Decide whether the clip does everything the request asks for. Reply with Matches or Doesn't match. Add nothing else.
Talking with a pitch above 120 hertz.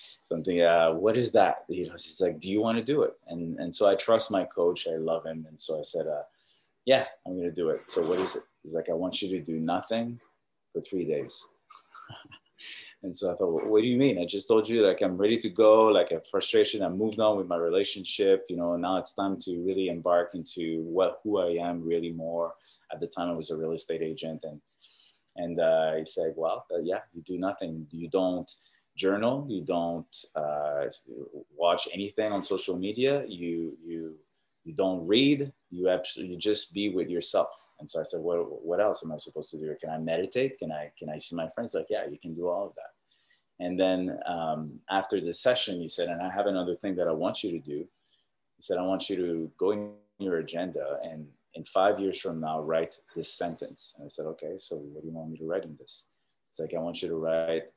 Doesn't match